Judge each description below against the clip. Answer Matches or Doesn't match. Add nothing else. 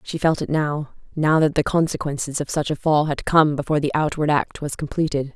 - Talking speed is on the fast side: Matches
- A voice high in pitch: Doesn't match